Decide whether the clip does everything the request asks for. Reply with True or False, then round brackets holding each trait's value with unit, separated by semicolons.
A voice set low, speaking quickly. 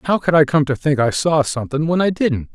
False (150 Hz; 285 wpm)